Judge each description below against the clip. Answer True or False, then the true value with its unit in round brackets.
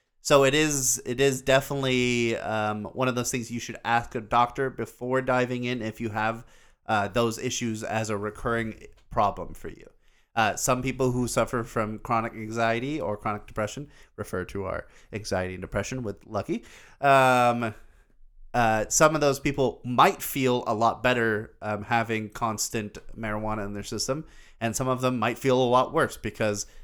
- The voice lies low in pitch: True (115 Hz)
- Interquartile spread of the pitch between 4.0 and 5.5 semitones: False (2.8 semitones)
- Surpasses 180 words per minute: False (175 wpm)